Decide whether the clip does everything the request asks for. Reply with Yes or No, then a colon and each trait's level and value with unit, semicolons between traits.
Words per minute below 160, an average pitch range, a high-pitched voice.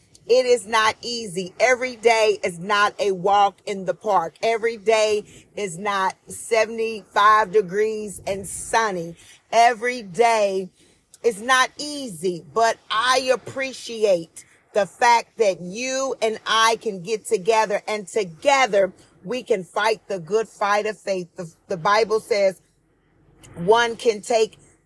Yes: slow, 135 wpm; average, 3.1 semitones; high, 215 Hz